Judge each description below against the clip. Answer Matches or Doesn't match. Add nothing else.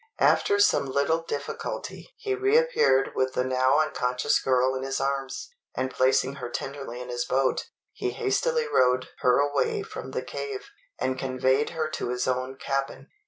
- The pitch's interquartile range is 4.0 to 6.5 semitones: Matches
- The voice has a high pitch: Doesn't match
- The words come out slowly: Doesn't match